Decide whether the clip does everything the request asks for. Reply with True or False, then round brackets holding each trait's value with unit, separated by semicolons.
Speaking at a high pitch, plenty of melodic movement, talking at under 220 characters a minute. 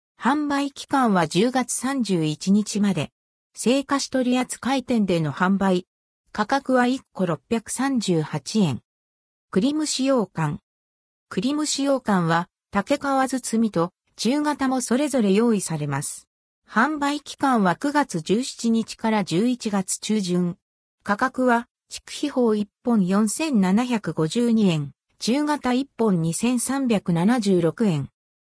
True (225 Hz; 6.5 semitones; 175 characters per minute)